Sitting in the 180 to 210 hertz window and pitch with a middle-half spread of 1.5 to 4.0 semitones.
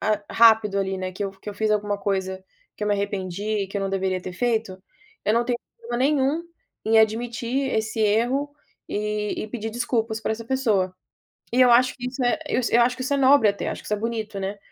No: high, 220 Hz; average, 3.1 semitones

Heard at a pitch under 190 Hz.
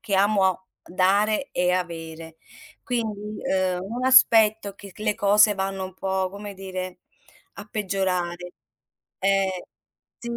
No: high, 195 Hz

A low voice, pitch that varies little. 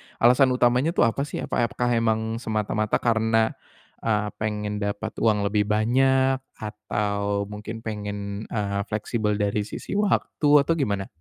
Yes: low, 110 Hz; narrow, 2.3 semitones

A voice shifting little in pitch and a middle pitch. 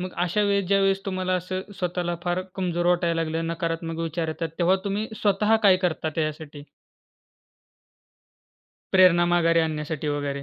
Yes: narrow, 2.3 semitones; medium, 175 Hz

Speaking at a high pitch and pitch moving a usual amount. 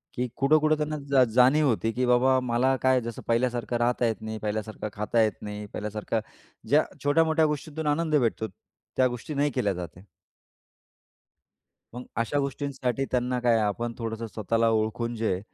No: low, 120 Hz; average, 3.7 semitones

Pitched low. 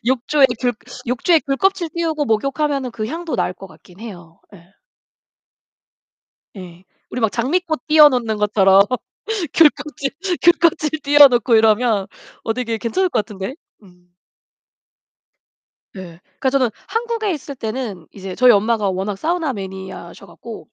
No: high, 245 Hz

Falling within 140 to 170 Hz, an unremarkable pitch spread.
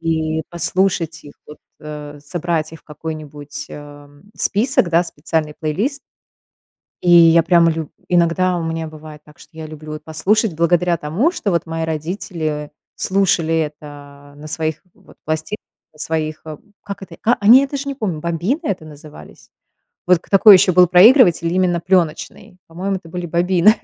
Yes: medium, 165 Hz; average, 3.0 semitones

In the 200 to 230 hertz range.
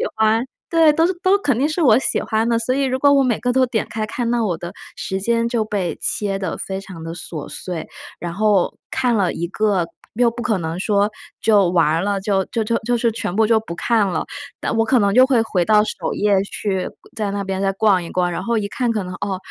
Yes: high, 215 Hz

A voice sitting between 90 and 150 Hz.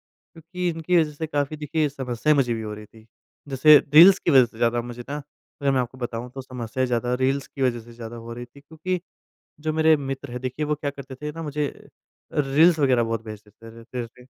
Yes: low, 135 Hz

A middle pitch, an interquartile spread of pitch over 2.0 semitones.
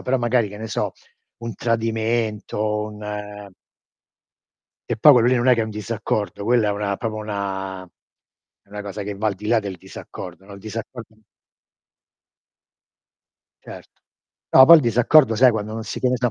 No: low, 110 Hz; narrow, 2.4 semitones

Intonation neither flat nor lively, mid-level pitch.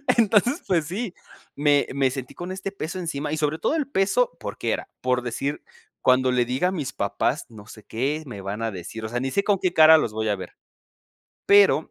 No: wide, 7.3 semitones; medium, 145 Hz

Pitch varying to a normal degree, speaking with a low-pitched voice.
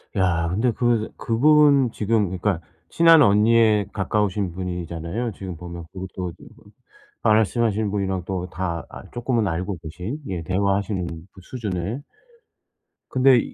Yes: average, 4.1 semitones; low, 100 Hz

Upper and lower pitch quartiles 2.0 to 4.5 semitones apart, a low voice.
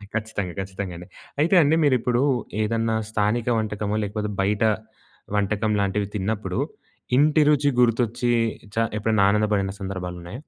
Yes: average, 2.9 semitones; low, 105 Hz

